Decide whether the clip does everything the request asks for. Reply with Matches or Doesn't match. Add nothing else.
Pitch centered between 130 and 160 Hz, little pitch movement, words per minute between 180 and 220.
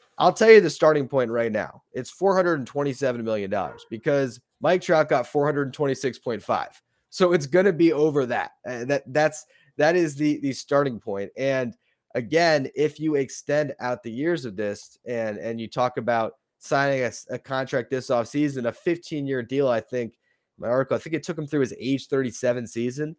Doesn't match